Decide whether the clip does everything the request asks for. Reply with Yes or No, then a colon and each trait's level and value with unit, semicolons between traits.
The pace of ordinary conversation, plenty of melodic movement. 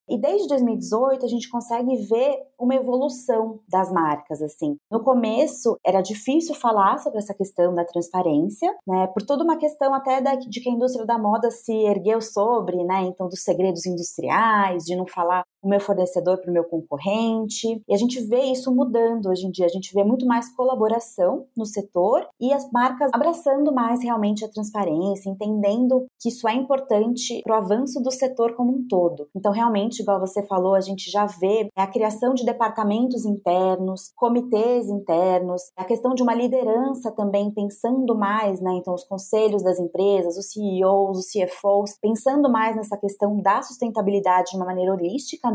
No: average, 175 wpm; average, 4.3 semitones